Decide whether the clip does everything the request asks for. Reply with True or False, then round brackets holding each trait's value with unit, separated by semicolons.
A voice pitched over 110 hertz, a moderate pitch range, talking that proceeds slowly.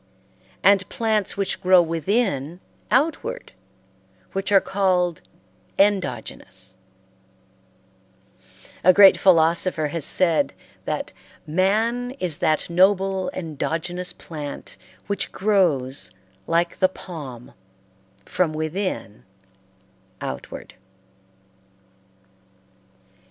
True (185 Hz; 3.5 semitones; 75 wpm)